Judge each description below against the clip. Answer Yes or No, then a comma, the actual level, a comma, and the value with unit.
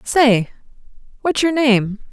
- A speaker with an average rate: No, slow, 115 wpm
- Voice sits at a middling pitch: No, very high, 250 Hz